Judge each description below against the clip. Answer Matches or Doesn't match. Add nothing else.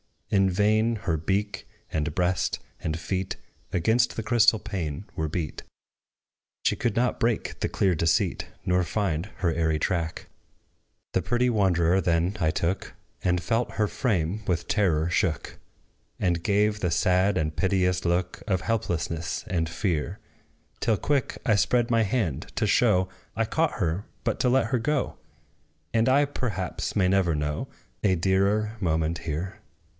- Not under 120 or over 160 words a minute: Matches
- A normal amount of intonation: Matches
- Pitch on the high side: Doesn't match